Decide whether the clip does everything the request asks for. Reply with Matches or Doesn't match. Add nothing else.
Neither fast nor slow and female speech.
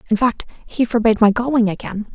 Matches